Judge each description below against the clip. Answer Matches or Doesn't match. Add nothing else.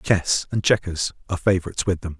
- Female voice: Doesn't match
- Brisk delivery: Doesn't match